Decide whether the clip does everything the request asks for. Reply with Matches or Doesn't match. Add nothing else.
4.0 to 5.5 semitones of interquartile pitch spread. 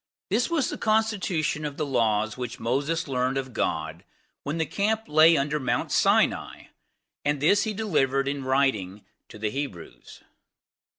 Matches